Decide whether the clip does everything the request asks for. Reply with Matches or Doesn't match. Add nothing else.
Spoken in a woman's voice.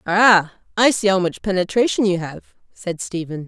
Matches